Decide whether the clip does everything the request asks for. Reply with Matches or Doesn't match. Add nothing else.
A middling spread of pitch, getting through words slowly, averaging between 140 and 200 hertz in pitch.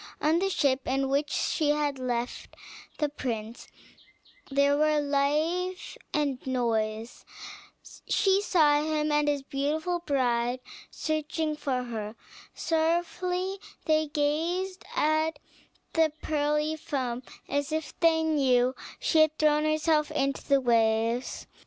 Doesn't match